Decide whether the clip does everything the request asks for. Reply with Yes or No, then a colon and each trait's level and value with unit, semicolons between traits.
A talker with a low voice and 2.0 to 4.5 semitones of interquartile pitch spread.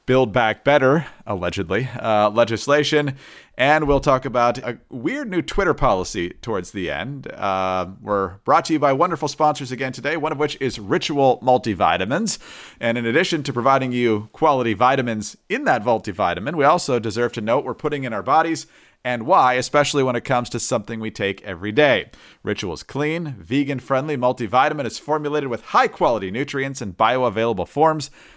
Yes: low, 130 Hz; average, 4.1 semitones